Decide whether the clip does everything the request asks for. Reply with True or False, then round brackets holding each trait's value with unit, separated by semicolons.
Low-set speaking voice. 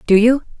False (230 Hz)